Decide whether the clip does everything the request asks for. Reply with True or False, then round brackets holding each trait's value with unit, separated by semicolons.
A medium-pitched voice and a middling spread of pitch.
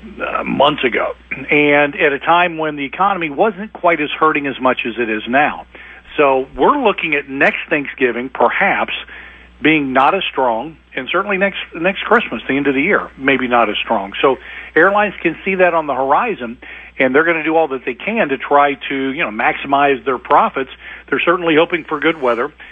True (145 Hz; 3.9 semitones)